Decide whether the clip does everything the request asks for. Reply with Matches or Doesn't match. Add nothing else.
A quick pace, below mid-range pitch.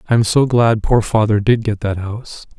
Matches